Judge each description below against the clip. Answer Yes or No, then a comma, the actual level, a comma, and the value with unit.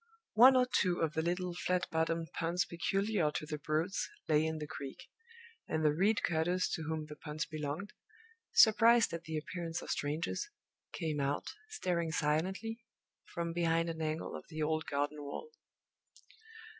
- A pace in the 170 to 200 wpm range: No, average, 160 wpm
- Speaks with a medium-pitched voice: Yes, medium, 165 Hz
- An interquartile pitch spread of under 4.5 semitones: Yes, average, 2.8 semitones